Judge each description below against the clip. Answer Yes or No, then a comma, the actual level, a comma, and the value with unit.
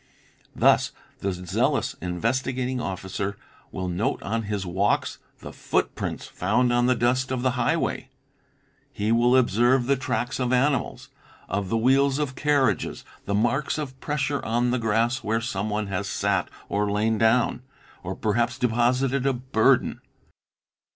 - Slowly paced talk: No, average, 145 wpm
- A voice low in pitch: Yes, low, 120 Hz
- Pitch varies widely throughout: No, average, 3.8 semitones